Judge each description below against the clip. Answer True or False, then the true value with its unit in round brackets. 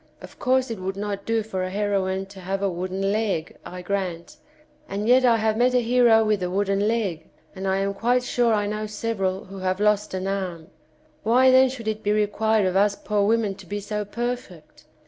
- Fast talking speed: True (215 wpm)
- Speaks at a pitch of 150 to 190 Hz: False (205 Hz)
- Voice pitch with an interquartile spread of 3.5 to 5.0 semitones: False (2.8 semitones)